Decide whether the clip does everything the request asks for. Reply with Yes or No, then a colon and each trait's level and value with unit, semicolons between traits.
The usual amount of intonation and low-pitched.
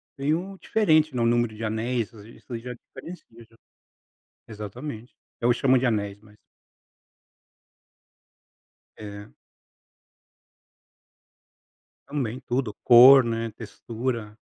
Yes: average, 3.0 semitones; low, 120 Hz